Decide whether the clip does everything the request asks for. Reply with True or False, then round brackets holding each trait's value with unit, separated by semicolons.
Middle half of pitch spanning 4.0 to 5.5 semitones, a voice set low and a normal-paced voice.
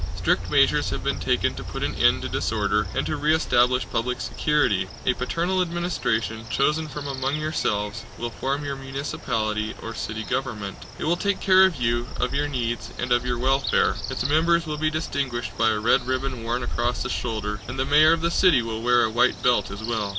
False (4.7 semitones; 125 Hz; 210 wpm)